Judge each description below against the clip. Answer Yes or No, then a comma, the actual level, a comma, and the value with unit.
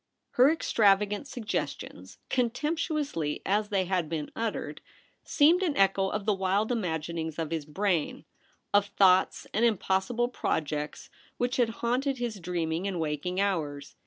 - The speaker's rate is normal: Yes, average, 145 wpm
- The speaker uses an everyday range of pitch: No, wide, 6.0 semitones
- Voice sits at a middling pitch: No, high, 195 Hz